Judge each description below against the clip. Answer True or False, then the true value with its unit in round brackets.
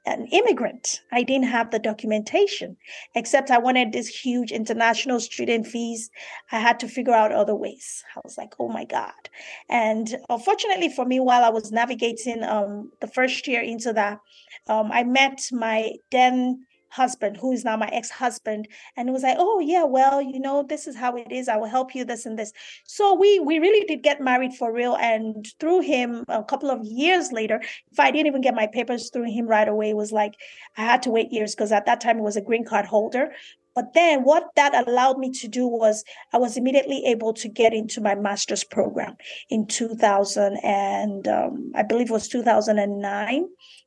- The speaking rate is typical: False (200 wpm)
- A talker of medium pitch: False (240 Hz)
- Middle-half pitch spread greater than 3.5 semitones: False (3.2 semitones)